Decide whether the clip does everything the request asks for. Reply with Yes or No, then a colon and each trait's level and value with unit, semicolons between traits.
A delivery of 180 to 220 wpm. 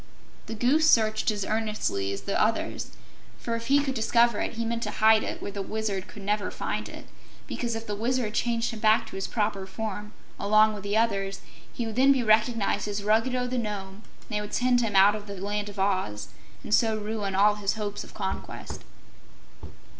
Yes: fast, 205 wpm